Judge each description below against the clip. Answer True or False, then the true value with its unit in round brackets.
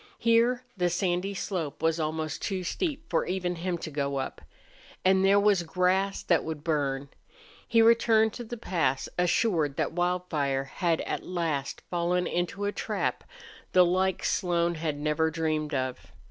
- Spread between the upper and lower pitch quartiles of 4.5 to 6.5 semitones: False (3.6 semitones)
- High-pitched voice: False (175 Hz)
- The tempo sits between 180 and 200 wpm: False (160 wpm)